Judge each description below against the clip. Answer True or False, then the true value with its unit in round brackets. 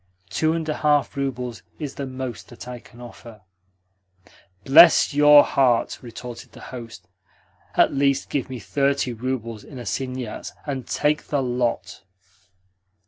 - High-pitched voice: False (130 Hz)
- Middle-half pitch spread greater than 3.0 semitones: False (2.7 semitones)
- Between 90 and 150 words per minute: True (140 wpm)